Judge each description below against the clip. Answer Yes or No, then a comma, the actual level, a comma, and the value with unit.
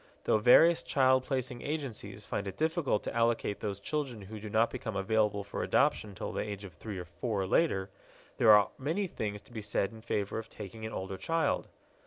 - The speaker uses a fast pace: Yes, fast, 210 wpm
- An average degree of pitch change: Yes, average, 4.2 semitones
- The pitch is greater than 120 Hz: No, low, 110 Hz